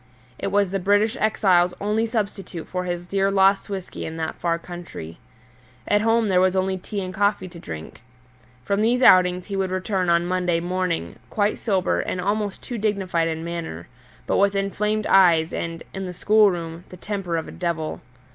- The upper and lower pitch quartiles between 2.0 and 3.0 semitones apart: Yes, average, 2.7 semitones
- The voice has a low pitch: No, medium, 185 Hz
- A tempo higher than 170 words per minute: Yes, average, 185 wpm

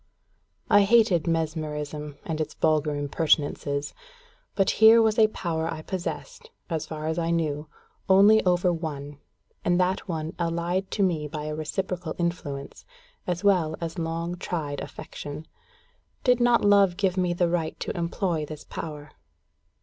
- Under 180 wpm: Yes, average, 150 wpm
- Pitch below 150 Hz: No, medium, 170 Hz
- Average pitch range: Yes, average, 3.3 semitones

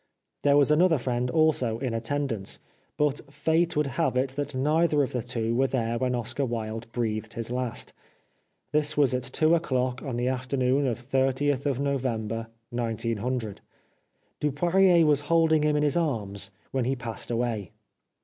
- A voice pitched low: Yes, low, 130 Hz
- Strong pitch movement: No, average, 3.8 semitones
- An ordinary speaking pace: Yes, average, 160 wpm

